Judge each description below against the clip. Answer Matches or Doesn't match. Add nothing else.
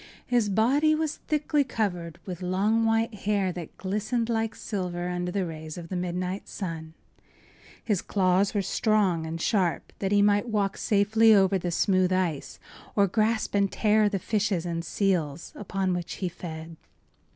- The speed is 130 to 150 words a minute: Doesn't match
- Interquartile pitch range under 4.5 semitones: Matches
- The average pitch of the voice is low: Doesn't match